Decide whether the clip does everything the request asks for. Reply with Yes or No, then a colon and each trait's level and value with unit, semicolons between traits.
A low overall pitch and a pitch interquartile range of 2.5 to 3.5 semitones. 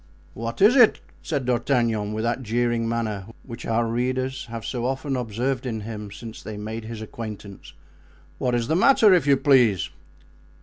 Yes: low, 120 Hz; average, 2.9 semitones